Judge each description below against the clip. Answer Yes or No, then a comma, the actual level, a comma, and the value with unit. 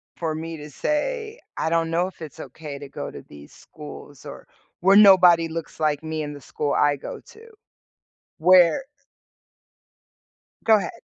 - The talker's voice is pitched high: No, medium, 165 Hz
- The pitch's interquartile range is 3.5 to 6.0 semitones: Yes, average, 4.1 semitones